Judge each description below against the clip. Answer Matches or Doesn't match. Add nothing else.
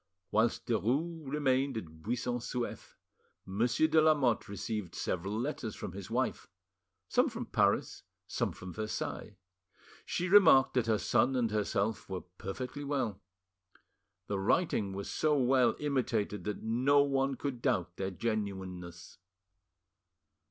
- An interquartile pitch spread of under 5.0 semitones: Doesn't match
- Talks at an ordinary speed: Doesn't match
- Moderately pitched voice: Doesn't match